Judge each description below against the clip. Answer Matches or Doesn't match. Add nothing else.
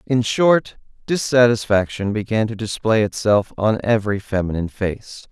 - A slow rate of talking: Matches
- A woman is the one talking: Doesn't match